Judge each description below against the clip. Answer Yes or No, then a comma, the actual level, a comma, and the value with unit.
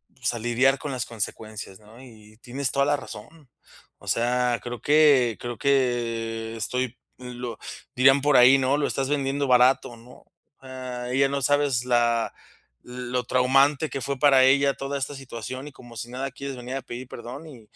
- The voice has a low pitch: Yes, low, 125 Hz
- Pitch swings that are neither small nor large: No, narrow, 2.3 semitones